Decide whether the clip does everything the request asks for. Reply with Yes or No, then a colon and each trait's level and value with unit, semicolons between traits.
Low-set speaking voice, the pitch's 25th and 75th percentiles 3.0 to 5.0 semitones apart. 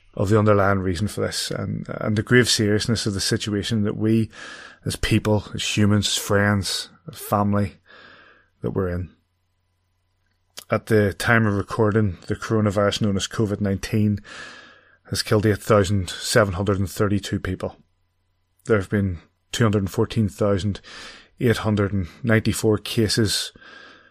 No: low, 105 Hz; narrow, 2.4 semitones